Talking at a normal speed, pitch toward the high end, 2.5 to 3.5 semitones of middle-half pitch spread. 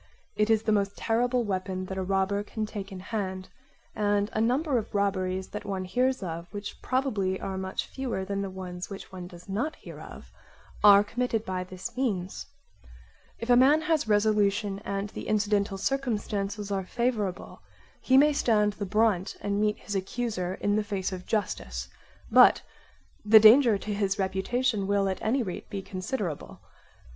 Yes: average, 170 wpm; high, 205 Hz; average, 2.8 semitones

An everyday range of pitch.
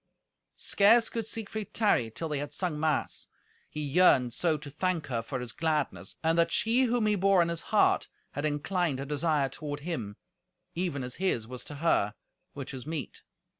Yes: average, 4.9 semitones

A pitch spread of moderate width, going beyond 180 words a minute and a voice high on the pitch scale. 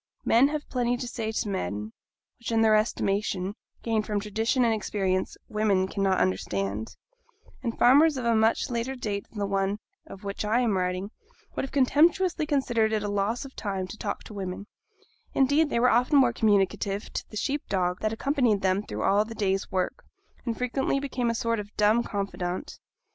Yes: average, 3.8 semitones; average, 190 wpm; high, 215 Hz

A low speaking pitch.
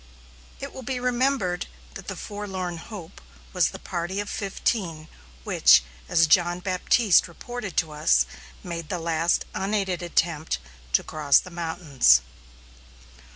No: medium, 175 Hz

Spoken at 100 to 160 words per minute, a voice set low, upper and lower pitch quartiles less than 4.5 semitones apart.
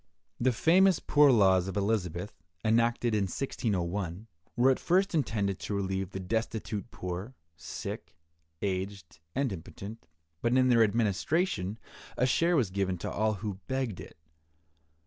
No: average, 140 wpm; low, 105 Hz; average, 4.8 semitones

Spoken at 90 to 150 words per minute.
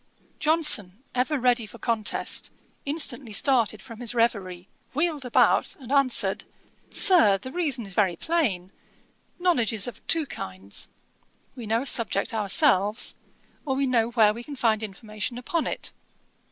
Yes: average, 145 wpm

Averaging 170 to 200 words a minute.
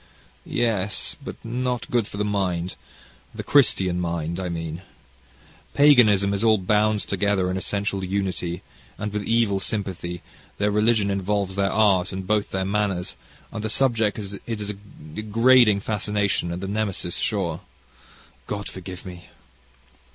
No: average, 140 wpm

